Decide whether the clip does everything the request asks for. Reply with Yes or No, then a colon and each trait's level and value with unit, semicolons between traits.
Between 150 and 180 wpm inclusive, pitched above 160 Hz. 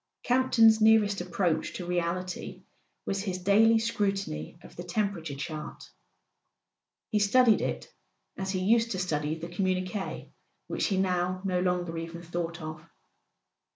No: slow, 135 wpm; medium, 185 Hz